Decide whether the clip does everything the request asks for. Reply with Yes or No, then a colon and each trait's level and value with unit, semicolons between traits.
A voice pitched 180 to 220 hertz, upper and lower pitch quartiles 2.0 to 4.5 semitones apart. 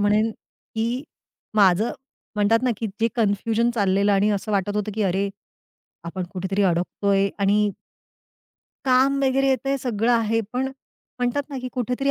Yes: high, 215 Hz; average, 3.6 semitones